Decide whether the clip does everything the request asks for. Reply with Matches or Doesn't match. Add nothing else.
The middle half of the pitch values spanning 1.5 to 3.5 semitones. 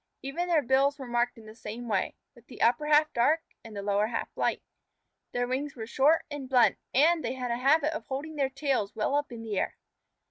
Doesn't match